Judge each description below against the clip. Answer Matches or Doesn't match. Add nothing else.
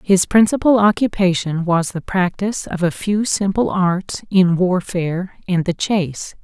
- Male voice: Doesn't match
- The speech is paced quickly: Doesn't match